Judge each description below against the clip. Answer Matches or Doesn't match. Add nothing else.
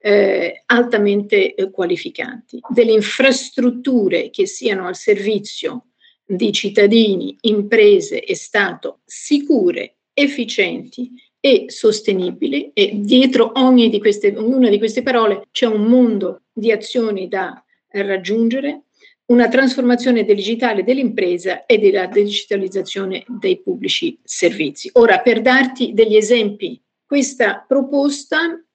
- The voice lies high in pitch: Matches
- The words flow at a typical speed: Doesn't match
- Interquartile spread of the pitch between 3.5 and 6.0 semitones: Matches